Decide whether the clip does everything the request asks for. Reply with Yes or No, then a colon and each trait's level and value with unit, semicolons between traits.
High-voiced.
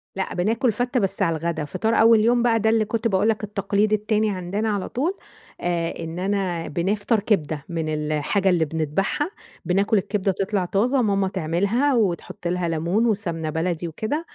Yes: high, 195 Hz